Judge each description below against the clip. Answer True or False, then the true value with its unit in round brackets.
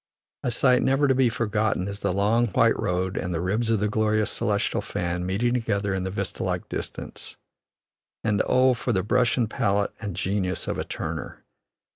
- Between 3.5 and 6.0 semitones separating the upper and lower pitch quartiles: True (3.8 semitones)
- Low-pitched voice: True (105 Hz)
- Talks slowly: False (190 wpm)